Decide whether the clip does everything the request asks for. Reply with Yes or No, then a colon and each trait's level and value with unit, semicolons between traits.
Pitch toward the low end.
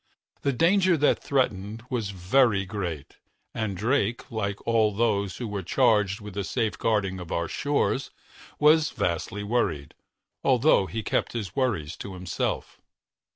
Yes: low, 105 Hz